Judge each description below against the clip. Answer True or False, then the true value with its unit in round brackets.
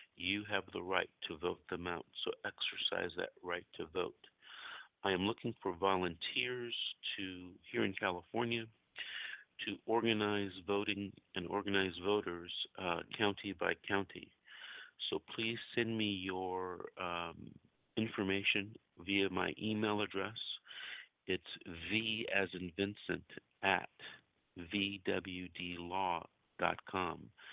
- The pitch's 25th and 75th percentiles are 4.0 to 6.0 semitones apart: False (3.2 semitones)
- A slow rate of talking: True (110 wpm)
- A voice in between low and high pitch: False (100 Hz)